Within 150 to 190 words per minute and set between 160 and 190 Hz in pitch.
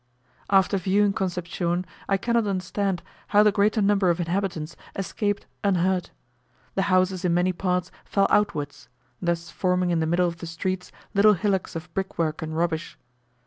Yes: average, 155 wpm; medium, 185 Hz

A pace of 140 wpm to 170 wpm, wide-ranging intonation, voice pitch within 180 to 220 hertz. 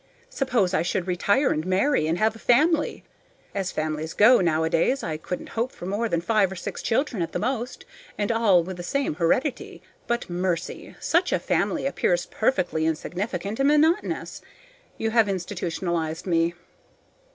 Yes: average, 165 wpm; wide, 5.7 semitones; high, 190 Hz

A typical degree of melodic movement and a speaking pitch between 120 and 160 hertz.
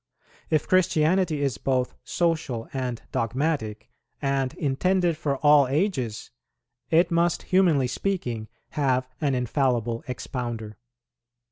Yes: average, 4.8 semitones; low, 135 Hz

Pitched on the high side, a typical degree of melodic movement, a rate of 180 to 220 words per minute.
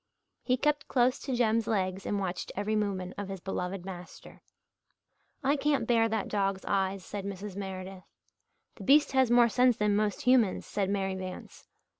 No: high, 205 Hz; average, 3.9 semitones; average, 170 wpm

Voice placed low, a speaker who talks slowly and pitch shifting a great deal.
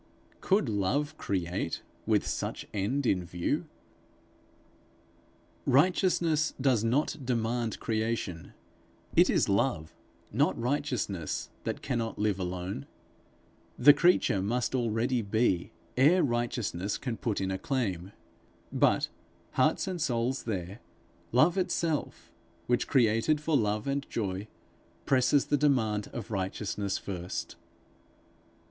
Yes: low, 115 Hz; slow, 110 wpm; wide, 5.7 semitones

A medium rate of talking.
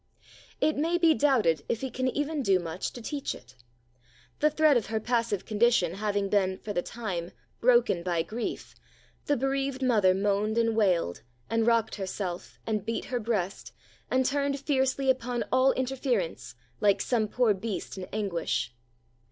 Yes: average, 160 wpm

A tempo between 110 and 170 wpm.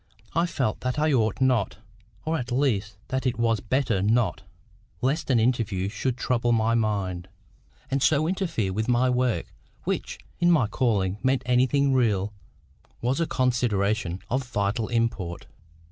Yes: average, 150 wpm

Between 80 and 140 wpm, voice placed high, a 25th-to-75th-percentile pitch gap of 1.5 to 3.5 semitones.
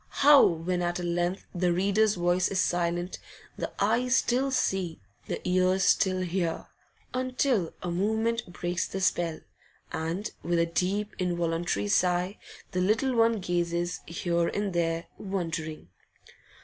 No: slow, 135 wpm; medium, 180 Hz; average, 2.9 semitones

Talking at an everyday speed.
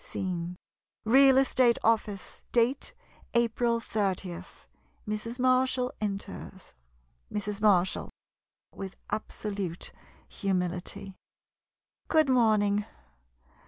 No: slow, 85 wpm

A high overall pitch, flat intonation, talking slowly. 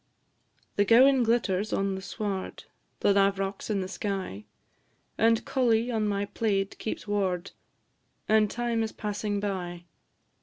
Yes: high, 205 Hz; narrow, 2.3 semitones; slow, 130 wpm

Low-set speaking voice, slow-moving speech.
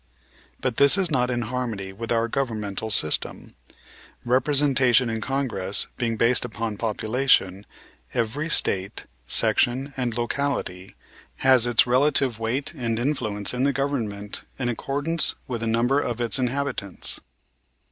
Yes: low, 120 Hz; slow, 130 wpm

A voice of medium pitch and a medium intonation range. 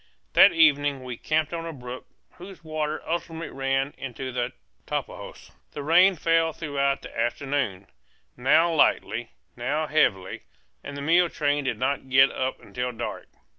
Yes: medium, 145 Hz; average, 3.7 semitones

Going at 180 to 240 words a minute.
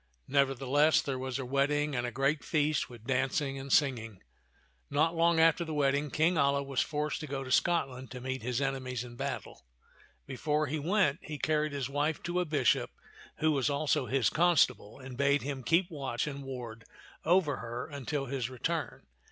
Yes: average, 185 wpm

